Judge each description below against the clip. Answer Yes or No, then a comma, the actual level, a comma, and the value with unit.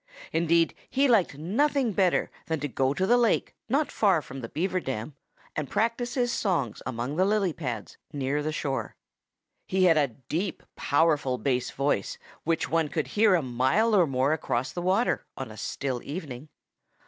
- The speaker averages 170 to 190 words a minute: Yes, average, 175 wpm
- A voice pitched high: No, medium, 160 Hz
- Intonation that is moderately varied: No, wide, 6.3 semitones